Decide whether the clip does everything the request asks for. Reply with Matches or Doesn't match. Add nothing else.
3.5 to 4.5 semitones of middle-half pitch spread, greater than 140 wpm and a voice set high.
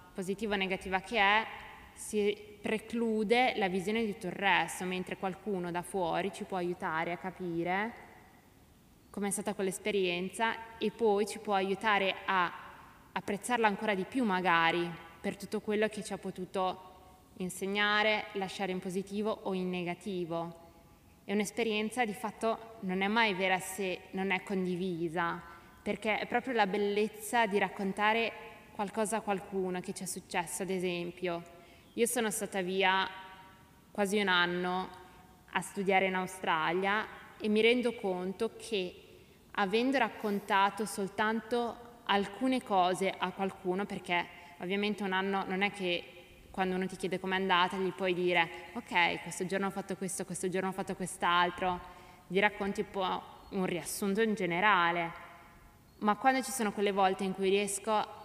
Doesn't match